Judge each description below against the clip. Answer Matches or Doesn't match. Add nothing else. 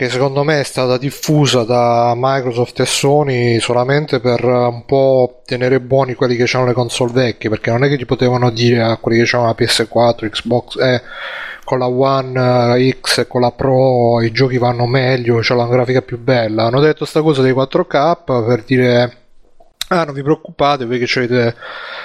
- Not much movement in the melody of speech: Matches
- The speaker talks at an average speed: Doesn't match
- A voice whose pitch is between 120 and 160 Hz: Matches